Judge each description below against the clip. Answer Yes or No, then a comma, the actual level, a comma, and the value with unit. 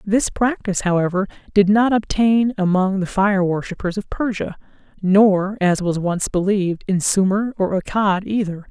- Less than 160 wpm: Yes, average, 150 wpm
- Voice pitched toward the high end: Yes, high, 195 Hz